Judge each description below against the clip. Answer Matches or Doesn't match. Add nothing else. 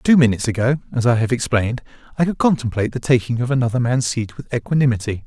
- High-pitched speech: Doesn't match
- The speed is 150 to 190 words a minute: Doesn't match